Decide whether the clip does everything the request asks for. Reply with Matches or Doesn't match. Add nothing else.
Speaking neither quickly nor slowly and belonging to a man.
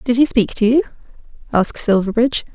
Doesn't match